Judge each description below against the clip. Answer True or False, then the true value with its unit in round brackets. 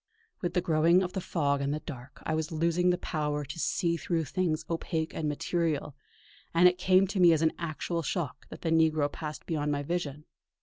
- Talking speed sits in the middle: False (210 wpm)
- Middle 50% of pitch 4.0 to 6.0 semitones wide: False (2.7 semitones)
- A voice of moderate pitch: True (160 Hz)